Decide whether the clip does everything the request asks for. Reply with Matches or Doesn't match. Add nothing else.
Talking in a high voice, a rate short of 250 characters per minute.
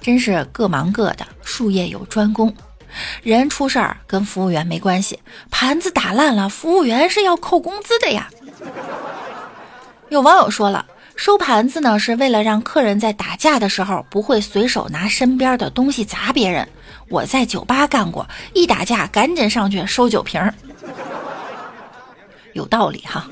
Matches